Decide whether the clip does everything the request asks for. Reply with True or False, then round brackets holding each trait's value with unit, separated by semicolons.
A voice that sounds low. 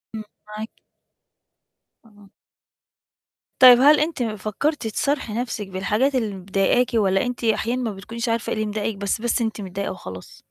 False (220 Hz)